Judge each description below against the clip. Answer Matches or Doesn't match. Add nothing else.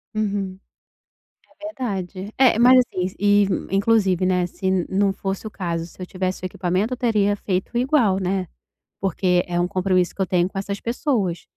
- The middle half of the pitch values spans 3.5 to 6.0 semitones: Doesn't match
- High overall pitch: Matches